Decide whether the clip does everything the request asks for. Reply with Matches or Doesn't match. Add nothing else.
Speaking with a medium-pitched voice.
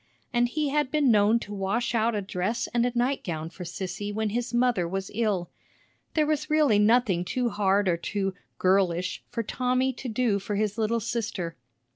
Doesn't match